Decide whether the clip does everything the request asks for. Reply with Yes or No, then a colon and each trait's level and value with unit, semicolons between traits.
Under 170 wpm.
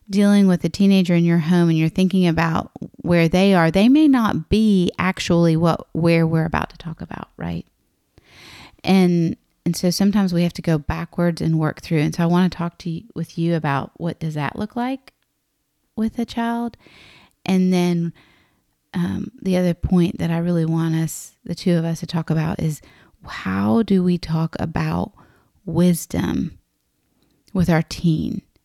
No: average, 180 wpm